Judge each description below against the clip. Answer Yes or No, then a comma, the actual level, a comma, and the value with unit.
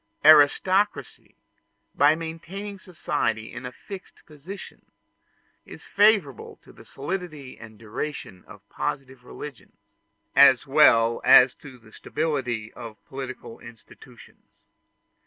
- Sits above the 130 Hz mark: Yes, medium, 140 Hz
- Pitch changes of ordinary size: No, wide, 5.8 semitones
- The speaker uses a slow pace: Yes, slow, 105 wpm